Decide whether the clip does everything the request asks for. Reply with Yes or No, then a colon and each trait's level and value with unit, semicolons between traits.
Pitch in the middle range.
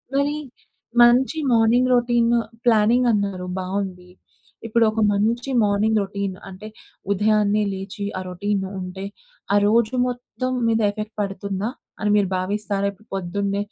No: high, 210 Hz